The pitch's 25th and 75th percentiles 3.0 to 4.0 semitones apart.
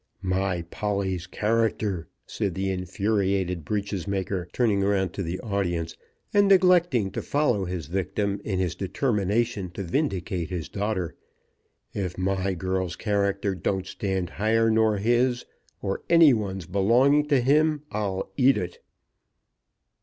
Yes: average, 3.4 semitones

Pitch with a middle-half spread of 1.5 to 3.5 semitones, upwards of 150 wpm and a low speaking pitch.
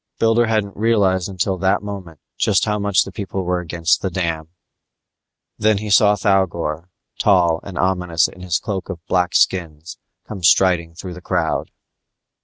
Yes: average, 2.8 semitones; average, 160 wpm; very low, 95 Hz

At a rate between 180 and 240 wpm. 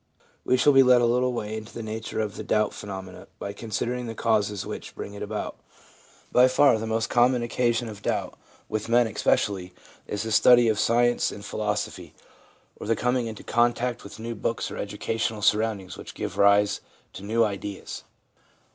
Yes: average, 185 wpm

